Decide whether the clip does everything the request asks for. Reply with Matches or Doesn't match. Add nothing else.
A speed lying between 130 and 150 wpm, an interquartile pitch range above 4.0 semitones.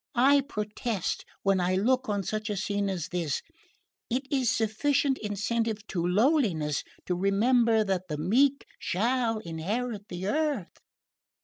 Matches